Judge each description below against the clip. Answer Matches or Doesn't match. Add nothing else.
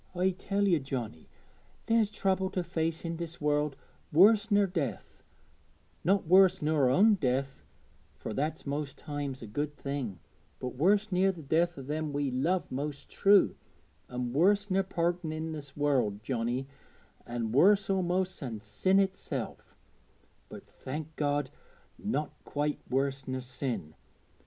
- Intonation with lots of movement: Matches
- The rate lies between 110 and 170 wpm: Matches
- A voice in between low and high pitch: Matches